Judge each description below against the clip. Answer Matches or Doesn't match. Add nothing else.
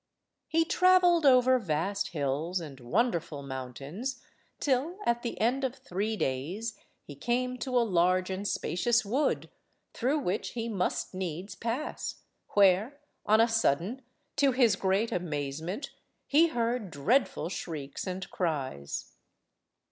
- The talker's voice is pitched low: Doesn't match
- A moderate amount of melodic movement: Doesn't match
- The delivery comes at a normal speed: Doesn't match